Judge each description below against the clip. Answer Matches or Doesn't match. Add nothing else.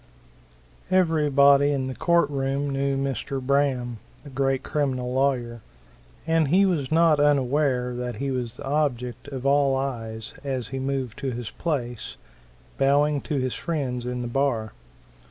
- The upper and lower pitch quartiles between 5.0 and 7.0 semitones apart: Doesn't match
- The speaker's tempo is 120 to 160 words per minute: Matches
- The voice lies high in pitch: Doesn't match